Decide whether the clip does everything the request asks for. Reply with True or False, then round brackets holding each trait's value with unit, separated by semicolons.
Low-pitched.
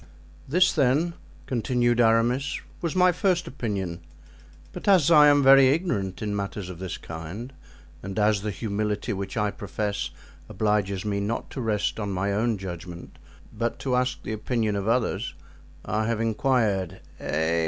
True (110 Hz)